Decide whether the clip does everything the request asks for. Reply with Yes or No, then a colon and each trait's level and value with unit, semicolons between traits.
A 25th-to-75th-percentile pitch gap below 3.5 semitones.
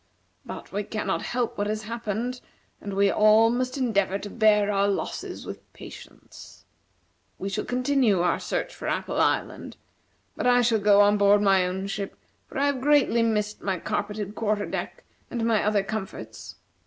Yes: narrow, 2.6 semitones